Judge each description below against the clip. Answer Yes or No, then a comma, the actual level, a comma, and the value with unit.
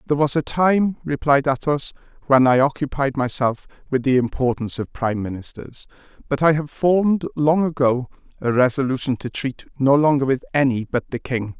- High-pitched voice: No, low, 135 Hz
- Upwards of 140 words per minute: Yes, average, 170 wpm